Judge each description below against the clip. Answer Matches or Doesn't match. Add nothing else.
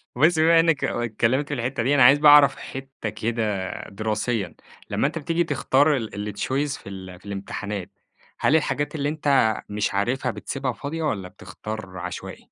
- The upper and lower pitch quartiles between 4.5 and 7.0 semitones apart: Matches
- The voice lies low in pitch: Matches